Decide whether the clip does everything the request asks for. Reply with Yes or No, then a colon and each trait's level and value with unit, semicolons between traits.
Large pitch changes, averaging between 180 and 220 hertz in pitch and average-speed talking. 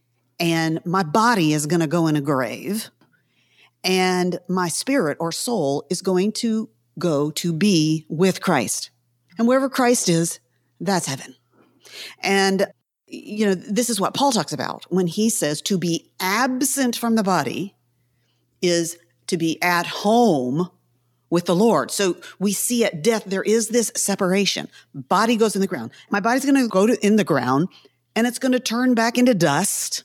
Yes: wide, 6.2 semitones; medium, 185 Hz; average, 170 wpm